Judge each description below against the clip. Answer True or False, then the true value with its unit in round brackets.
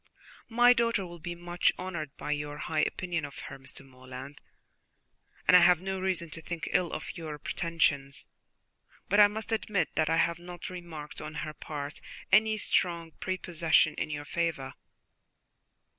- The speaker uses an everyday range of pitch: True (3.5 semitones)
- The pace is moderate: True (160 wpm)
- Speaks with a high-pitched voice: False (170 Hz)